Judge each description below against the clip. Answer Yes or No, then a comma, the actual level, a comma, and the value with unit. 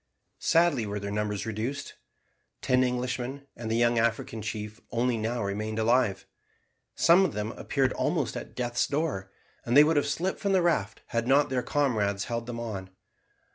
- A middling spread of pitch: Yes, average, 4.4 semitones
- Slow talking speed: No, average, 175 wpm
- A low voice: Yes, low, 120 Hz